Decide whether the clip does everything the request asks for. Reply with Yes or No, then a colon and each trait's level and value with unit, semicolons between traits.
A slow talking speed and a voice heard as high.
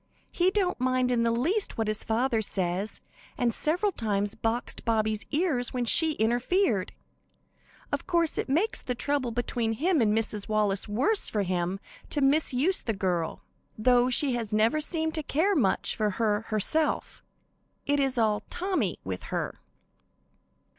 No: average, 155 wpm; high, 240 Hz